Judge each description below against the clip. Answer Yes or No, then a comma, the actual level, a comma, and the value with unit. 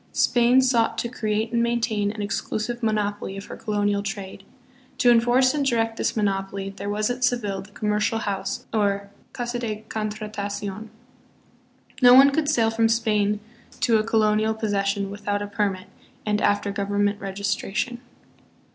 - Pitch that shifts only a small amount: Yes, narrow, 2.3 semitones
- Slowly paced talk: No, average, 150 wpm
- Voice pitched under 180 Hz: No, high, 215 Hz